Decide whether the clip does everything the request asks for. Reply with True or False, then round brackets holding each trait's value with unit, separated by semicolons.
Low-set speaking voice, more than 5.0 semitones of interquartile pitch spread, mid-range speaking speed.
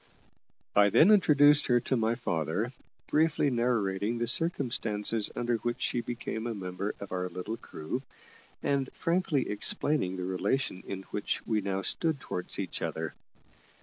True (115 Hz; 5.6 semitones; 150 wpm)